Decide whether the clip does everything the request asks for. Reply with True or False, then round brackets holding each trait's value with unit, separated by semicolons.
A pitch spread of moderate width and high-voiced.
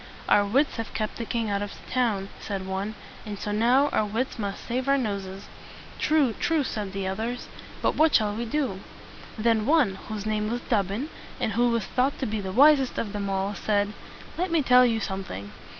True (3.9 semitones; 220 Hz)